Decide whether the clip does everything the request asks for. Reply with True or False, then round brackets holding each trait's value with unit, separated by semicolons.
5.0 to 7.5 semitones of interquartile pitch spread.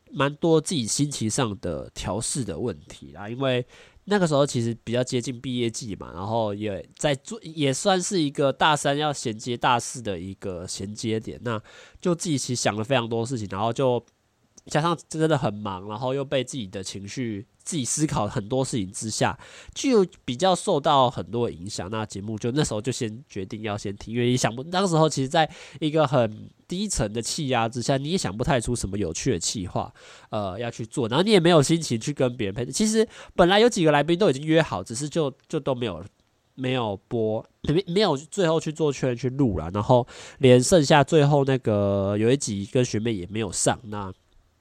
True (5.6 semitones)